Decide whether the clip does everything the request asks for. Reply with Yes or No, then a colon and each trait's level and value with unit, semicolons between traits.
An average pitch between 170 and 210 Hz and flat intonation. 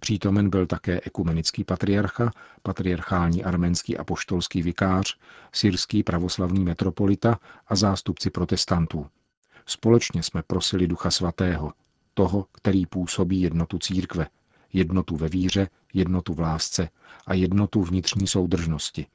No: very low, 95 Hz; narrow, 2.0 semitones